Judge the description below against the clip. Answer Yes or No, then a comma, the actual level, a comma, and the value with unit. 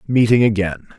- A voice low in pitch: Yes, low, 110 Hz